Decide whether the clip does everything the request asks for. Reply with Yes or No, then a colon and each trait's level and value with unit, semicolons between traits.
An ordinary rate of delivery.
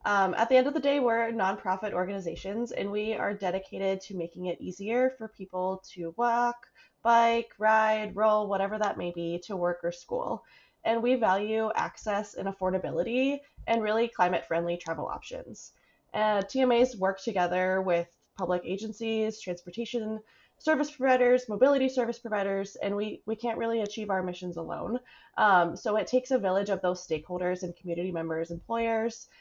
Yes: average, 165 wpm